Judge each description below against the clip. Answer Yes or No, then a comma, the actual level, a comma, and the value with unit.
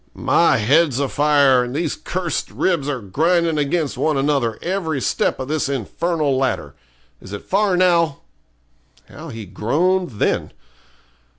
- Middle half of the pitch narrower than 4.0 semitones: No, average, 4.4 semitones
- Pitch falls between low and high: Yes, medium, 150 Hz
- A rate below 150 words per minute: Yes, average, 140 wpm